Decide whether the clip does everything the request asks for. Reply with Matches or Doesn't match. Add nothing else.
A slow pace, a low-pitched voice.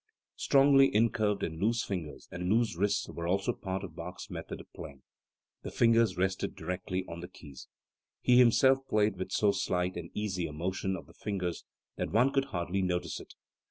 Doesn't match